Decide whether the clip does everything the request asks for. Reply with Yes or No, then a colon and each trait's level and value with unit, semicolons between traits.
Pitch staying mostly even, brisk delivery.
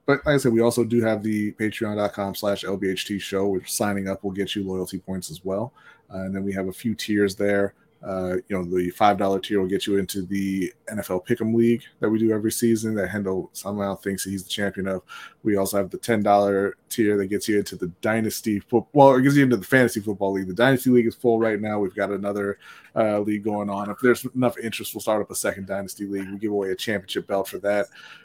Yes: narrow, 2.2 semitones; fast, 245 wpm